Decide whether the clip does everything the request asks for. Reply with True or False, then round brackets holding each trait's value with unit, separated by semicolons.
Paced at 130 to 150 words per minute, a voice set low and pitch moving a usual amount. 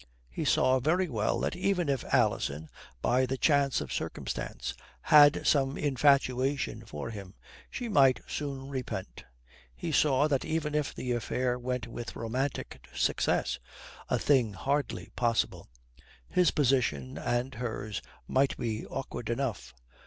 True (135 wpm; 130 Hz; 3.6 semitones)